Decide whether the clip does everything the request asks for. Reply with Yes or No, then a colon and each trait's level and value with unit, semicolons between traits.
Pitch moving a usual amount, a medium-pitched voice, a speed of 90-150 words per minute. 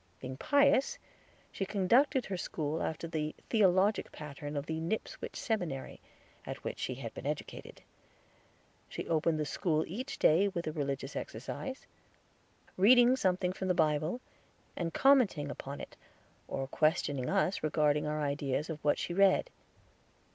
Yes: average, 5.0 semitones; medium, 165 Hz; average, 145 wpm